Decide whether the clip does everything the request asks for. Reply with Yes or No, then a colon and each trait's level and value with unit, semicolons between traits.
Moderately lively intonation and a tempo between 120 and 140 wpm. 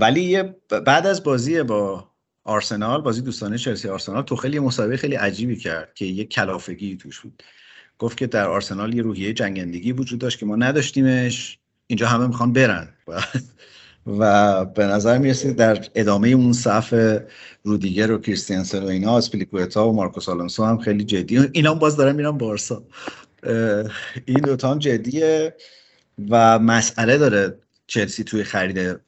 No: average, 3.9 semitones; fast, 155 wpm